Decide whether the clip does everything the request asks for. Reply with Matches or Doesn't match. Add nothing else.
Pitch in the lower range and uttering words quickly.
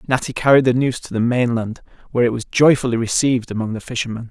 Matches